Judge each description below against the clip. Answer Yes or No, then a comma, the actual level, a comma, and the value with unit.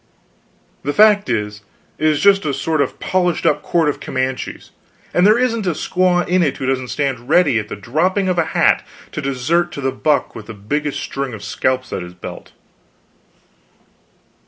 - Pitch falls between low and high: Yes, medium, 145 Hz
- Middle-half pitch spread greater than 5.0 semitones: Yes, wide, 5.6 semitones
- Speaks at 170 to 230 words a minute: Yes, average, 185 wpm